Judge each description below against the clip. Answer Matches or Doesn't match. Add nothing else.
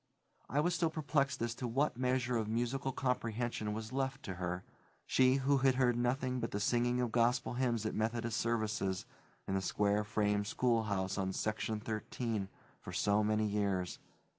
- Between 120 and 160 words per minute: Doesn't match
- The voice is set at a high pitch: Doesn't match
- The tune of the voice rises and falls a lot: Doesn't match